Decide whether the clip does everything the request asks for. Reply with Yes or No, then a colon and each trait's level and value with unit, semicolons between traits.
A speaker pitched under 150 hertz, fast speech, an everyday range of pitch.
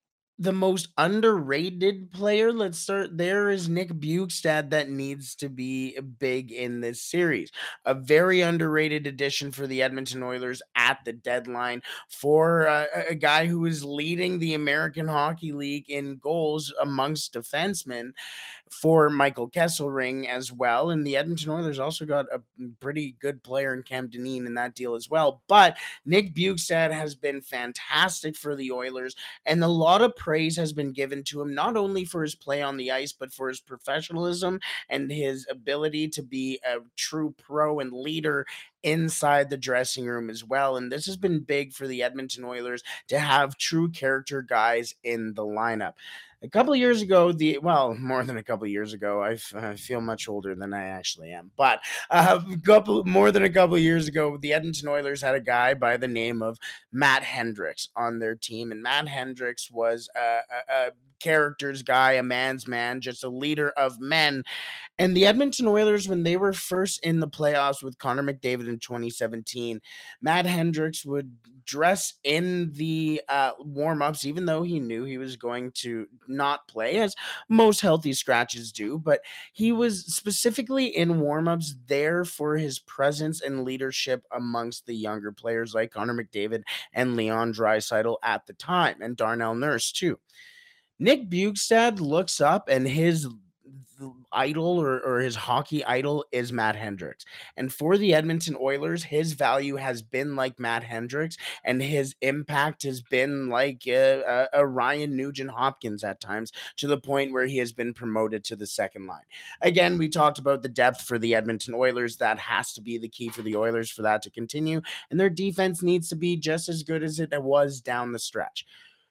No: medium, 140 Hz; average, 180 wpm; average, 4.6 semitones